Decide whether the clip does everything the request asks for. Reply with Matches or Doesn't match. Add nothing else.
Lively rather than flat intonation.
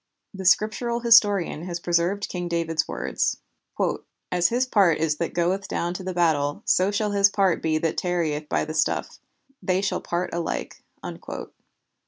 Doesn't match